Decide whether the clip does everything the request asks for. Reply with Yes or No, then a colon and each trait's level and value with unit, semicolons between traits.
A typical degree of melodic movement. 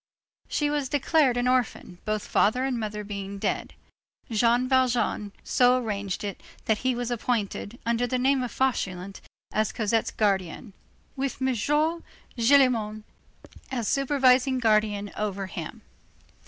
Yes: average, 3.6 semitones